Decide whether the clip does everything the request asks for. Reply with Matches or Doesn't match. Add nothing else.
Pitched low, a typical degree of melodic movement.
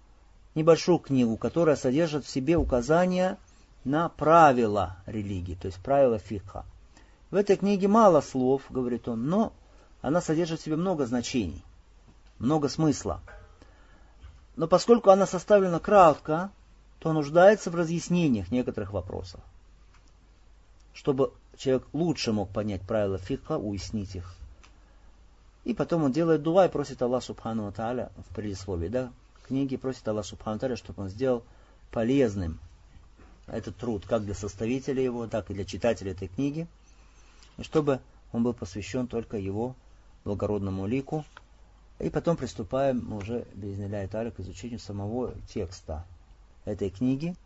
Doesn't match